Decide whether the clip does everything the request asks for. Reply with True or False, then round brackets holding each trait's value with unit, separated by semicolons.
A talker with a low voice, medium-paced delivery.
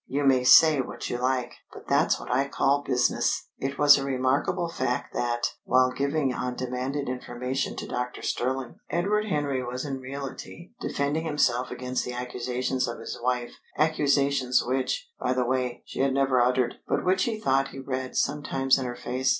True (130 Hz; 175 wpm)